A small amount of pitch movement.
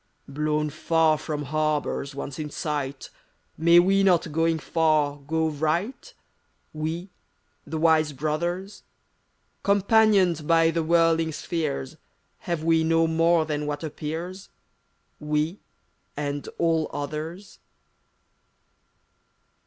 Yes: narrow, 2.0 semitones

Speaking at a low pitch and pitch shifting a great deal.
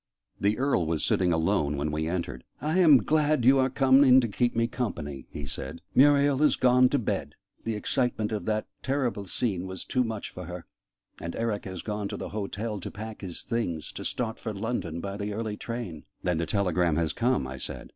Yes: low, 105 Hz; wide, 6.3 semitones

